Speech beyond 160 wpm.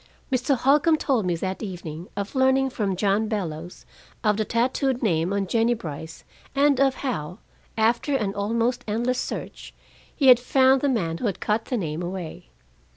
Yes: average, 170 wpm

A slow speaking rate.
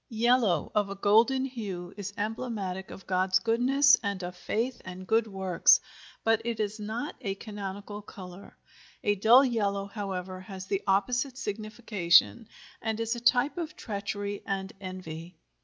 No: average, 150 wpm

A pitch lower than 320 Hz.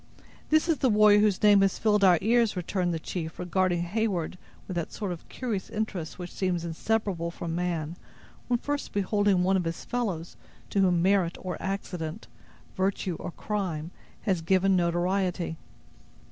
Yes: medium, 185 Hz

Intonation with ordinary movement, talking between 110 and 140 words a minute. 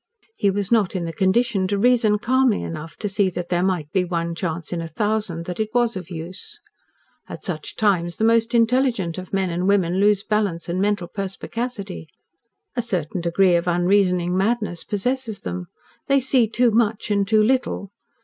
No: average, 4.0 semitones; average, 185 wpm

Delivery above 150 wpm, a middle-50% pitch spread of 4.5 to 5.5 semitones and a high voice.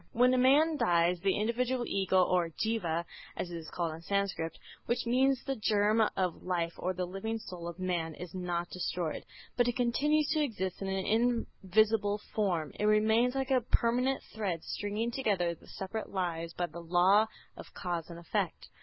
Yes: average, 180 wpm; average, 5.1 semitones; high, 195 Hz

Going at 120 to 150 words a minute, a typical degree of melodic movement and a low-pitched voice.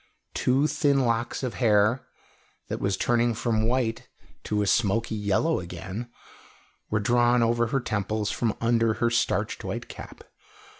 No: average, 145 wpm; narrow, 2.3 semitones; low, 115 Hz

